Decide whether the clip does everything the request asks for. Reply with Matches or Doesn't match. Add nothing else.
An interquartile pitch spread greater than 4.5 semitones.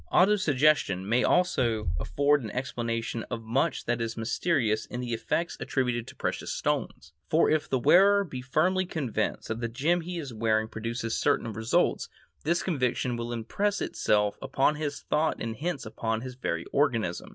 Matches